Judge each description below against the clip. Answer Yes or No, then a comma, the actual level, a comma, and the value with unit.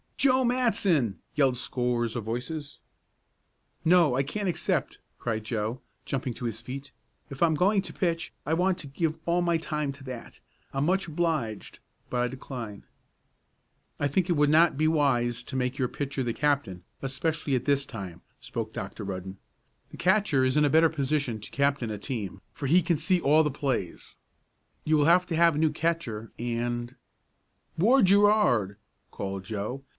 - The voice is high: No, medium, 140 Hz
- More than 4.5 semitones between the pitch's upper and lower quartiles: Yes, wide, 5.5 semitones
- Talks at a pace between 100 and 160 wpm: No, average, 175 wpm